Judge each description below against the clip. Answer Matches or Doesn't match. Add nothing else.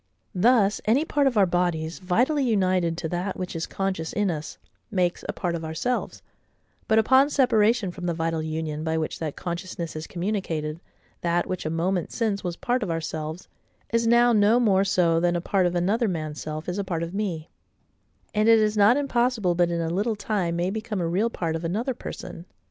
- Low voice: Doesn't match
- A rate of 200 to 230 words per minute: Matches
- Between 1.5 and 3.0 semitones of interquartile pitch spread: Doesn't match